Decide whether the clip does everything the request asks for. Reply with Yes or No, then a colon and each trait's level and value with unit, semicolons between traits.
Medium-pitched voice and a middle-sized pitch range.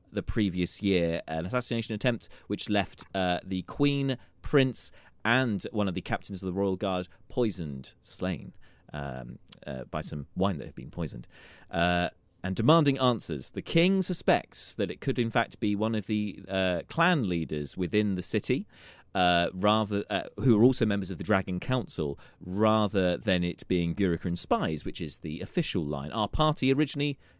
No: low, 100 Hz; average, 4.7 semitones